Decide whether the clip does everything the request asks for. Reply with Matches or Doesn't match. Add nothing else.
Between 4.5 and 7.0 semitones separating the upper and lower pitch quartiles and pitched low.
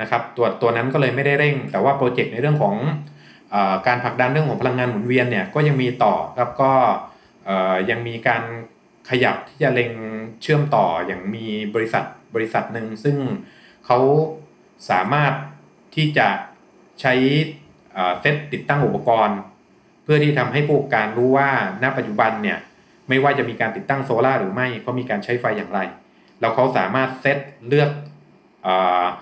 Doesn't match